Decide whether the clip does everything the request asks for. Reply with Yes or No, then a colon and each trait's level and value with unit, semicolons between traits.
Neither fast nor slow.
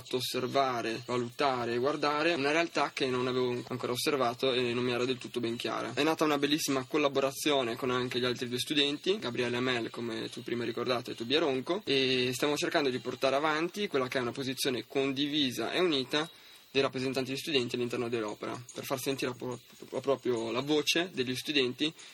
No: fast, 180 wpm